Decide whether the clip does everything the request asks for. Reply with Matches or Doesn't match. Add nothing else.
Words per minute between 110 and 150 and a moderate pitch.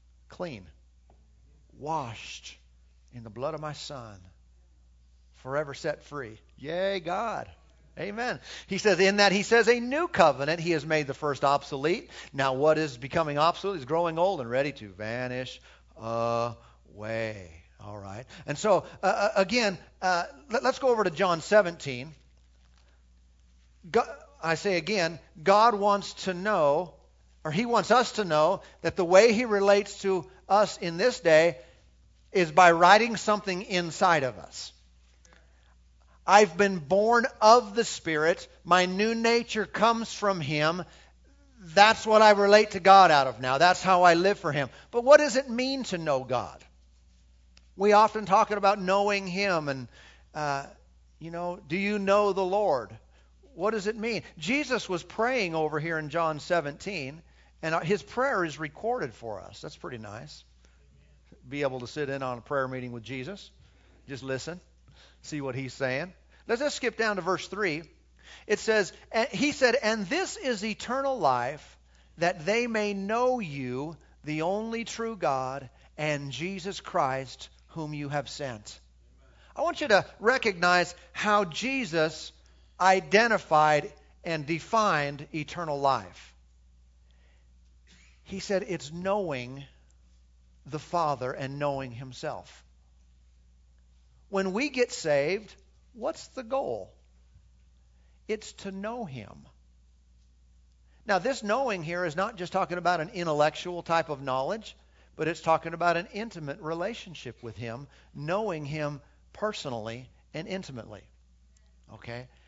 Matches